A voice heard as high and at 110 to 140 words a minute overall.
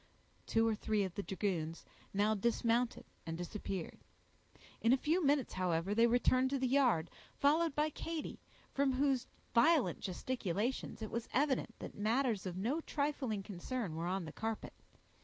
No: high, 230 Hz; average, 160 wpm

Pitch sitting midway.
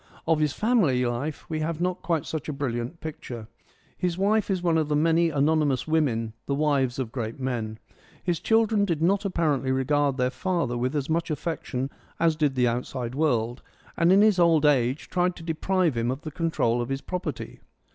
Yes: medium, 150 Hz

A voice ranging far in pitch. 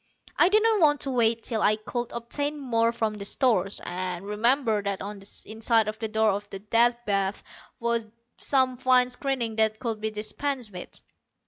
No: average, 3.2 semitones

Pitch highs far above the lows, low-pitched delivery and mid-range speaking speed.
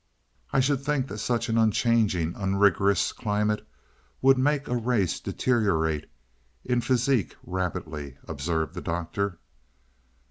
No: wide, 6.1 semitones; low, 105 Hz; slow, 115 wpm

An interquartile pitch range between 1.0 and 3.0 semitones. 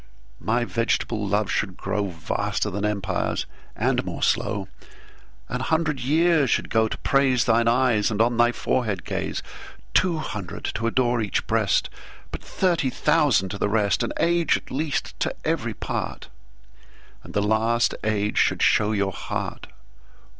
No: average, 4.0 semitones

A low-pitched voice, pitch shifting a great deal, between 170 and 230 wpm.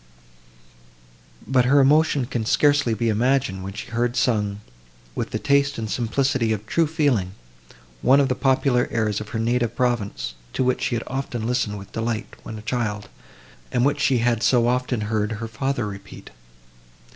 No: low, 120 Hz; average, 3.7 semitones; average, 180 wpm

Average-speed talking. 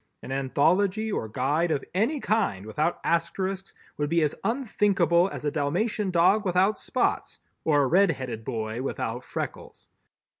Yes: average, 150 wpm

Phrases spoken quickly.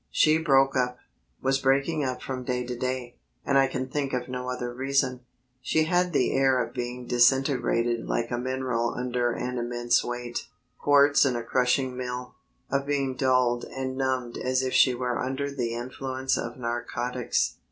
No: average, 175 wpm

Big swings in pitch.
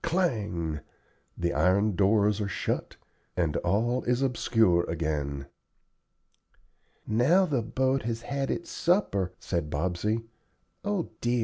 Yes: wide, 6.8 semitones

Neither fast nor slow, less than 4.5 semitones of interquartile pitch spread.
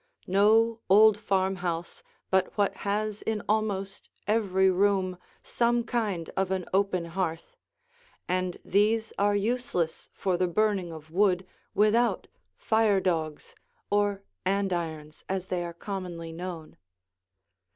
No: slow, 120 wpm; average, 2.7 semitones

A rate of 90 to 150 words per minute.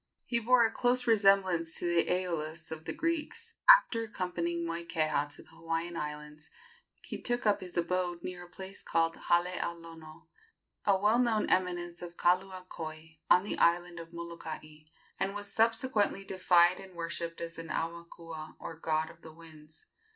No: average, 165 wpm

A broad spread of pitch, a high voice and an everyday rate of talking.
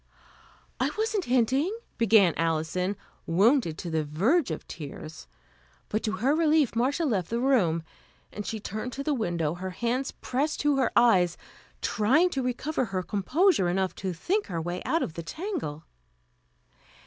Yes: wide, 7.9 semitones; high, 225 Hz; average, 160 wpm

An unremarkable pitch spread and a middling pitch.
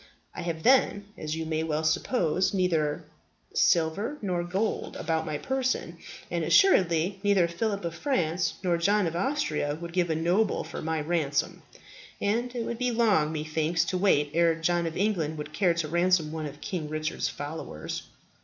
Yes: average, 3.9 semitones; medium, 170 Hz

